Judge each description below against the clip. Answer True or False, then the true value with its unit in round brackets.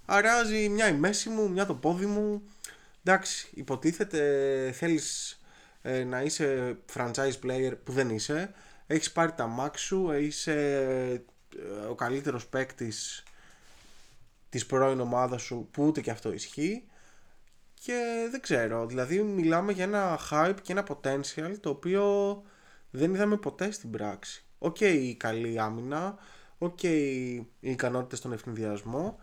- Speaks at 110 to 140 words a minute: True (135 wpm)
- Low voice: False (145 Hz)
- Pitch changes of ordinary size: False (7.1 semitones)